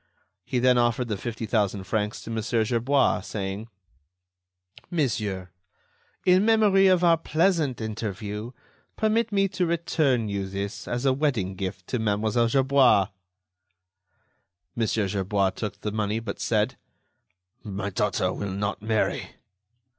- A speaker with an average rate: No, slow, 130 wpm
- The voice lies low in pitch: Yes, low, 110 Hz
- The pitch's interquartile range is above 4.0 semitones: Yes, average, 5.2 semitones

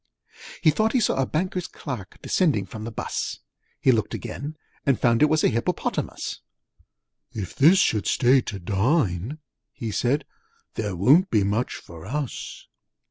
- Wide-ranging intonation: Yes, wide, 6.5 semitones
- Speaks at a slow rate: No, average, 155 wpm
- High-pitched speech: No, low, 125 Hz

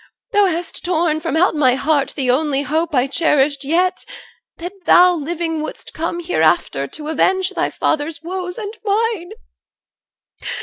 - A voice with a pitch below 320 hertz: No, very high, 325 Hz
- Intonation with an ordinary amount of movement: Yes, average, 3.6 semitones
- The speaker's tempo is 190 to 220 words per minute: No, average, 145 wpm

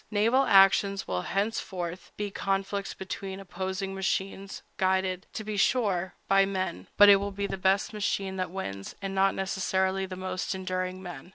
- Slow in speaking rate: No, average, 165 wpm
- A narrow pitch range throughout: Yes, narrow, 1.0 semitones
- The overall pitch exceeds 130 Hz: Yes, high, 190 Hz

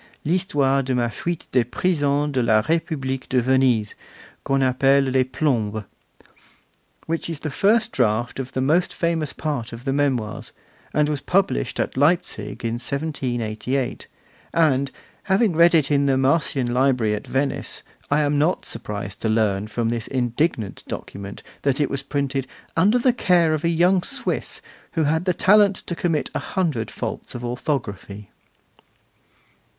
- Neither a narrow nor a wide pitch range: Yes, average, 5.0 semitones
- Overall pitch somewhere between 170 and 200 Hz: No, low, 135 Hz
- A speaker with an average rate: Yes, average, 155 wpm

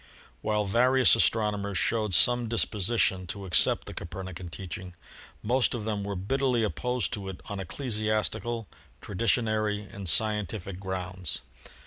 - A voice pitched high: No, low, 105 Hz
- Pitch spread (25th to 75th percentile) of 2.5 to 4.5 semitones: Yes, average, 3.3 semitones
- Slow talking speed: Yes, slow, 125 wpm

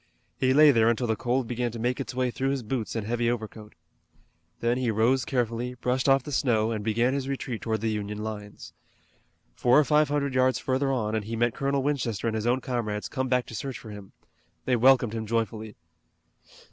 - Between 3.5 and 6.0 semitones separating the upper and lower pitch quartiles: No, average, 2.9 semitones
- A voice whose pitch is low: Yes, low, 120 Hz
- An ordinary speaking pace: No, fast, 210 wpm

